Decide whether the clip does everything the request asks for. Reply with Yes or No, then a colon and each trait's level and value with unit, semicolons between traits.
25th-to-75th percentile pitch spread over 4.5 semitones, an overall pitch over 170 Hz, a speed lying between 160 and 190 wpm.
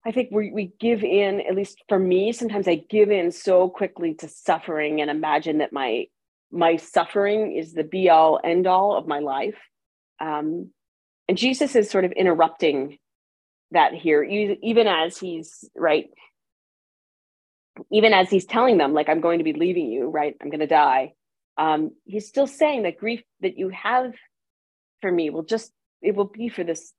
Yes: average, 4.9 semitones; medium, 185 Hz; average, 175 wpm